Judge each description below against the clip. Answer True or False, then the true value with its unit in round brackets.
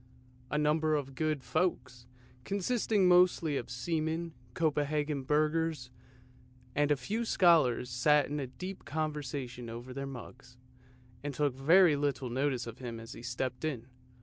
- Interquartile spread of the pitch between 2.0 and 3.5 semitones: False (3.9 semitones)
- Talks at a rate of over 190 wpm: False (140 wpm)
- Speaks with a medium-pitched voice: True (145 Hz)